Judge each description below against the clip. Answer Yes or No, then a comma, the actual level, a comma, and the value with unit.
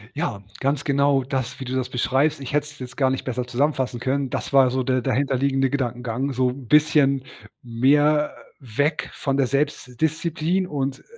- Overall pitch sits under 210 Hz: Yes, low, 135 Hz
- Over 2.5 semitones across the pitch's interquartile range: No, narrow, 2.2 semitones